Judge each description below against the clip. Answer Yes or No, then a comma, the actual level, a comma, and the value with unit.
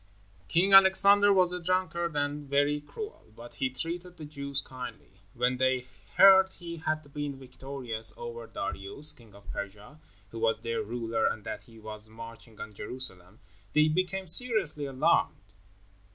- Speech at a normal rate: Yes, average, 150 wpm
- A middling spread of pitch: No, wide, 6.9 semitones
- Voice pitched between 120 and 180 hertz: Yes, medium, 140 Hz